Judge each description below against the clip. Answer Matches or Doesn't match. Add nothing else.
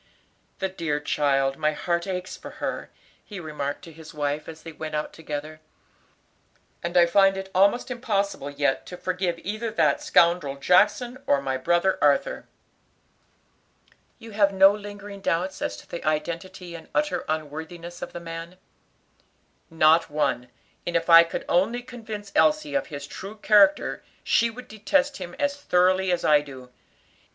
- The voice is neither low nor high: Matches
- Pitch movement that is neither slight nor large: Matches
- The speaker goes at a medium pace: Matches